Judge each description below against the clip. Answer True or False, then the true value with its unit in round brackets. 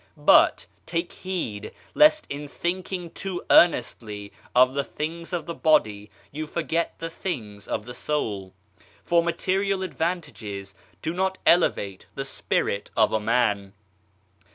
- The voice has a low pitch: False (155 Hz)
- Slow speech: True (130 wpm)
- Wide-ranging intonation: True (8.5 semitones)